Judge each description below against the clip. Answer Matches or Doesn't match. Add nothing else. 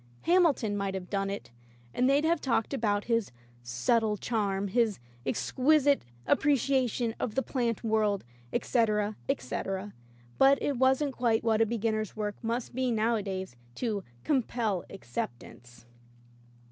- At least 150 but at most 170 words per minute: Doesn't match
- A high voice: Matches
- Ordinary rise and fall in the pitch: Matches